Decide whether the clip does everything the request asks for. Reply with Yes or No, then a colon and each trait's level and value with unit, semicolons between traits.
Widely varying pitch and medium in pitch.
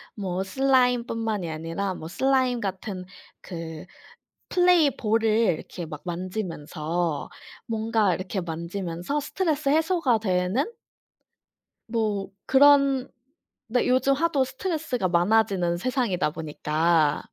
No: wide, 7.0 semitones; high, 215 Hz